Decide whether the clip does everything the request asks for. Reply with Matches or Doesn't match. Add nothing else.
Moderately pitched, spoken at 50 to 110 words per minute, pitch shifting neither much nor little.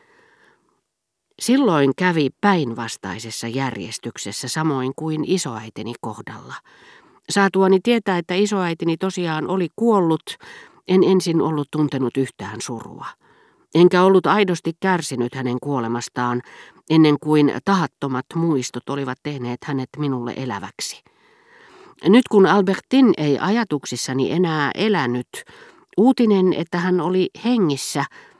Doesn't match